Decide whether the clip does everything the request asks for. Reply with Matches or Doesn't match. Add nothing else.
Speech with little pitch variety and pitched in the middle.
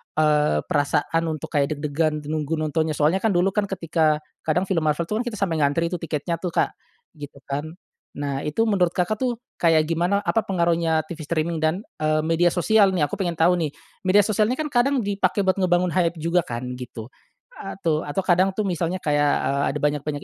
Doesn't match